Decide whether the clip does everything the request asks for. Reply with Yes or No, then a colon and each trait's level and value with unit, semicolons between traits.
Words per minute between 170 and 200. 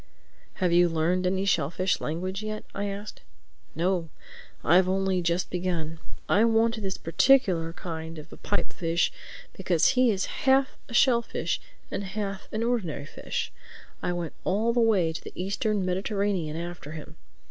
No: average, 155 wpm